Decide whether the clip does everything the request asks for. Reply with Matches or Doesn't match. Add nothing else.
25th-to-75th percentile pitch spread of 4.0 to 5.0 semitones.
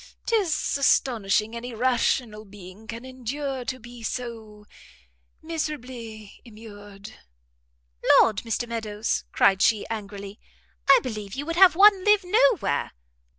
Matches